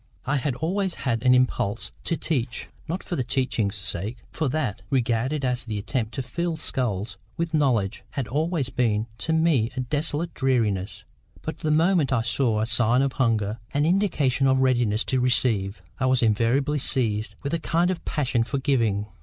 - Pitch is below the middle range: Yes, low, 130 Hz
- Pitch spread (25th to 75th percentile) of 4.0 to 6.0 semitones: Yes, average, 4.7 semitones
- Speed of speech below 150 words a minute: No, average, 180 wpm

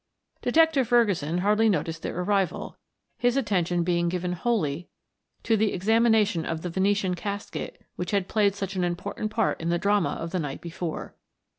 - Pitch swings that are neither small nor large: Yes, average, 3.7 semitones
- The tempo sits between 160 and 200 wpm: Yes, average, 165 wpm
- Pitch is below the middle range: No, high, 190 Hz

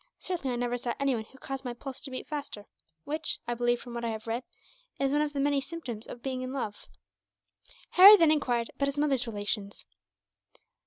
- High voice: Yes, very high, 255 Hz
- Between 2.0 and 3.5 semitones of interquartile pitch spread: Yes, average, 3.1 semitones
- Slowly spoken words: No, fast, 205 wpm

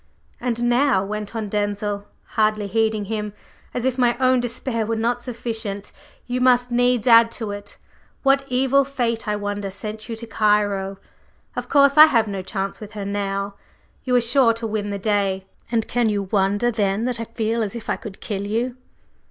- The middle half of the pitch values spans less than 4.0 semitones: Yes, average, 3.0 semitones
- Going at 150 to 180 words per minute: No, average, 190 wpm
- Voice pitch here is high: Yes, high, 220 Hz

